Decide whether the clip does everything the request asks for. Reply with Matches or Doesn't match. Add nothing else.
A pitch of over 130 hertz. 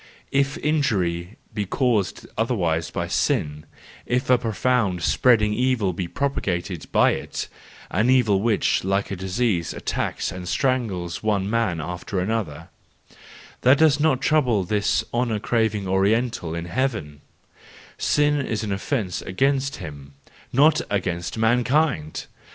Doesn't match